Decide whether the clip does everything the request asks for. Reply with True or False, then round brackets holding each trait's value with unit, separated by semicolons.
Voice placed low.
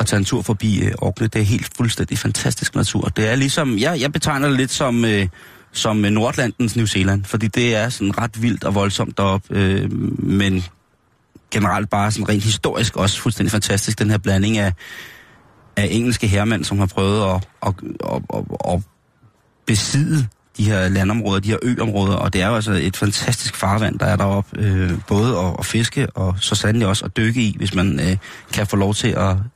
True (105 Hz)